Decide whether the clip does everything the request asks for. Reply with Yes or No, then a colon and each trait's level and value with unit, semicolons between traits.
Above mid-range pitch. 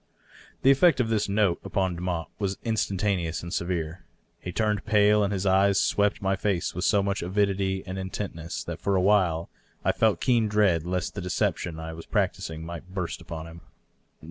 No: very low, 95 Hz